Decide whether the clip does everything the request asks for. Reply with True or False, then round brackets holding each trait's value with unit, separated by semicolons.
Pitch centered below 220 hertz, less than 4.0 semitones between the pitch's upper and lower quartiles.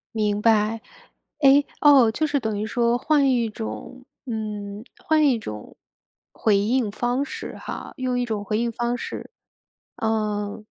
False (225 Hz; 3.3 semitones)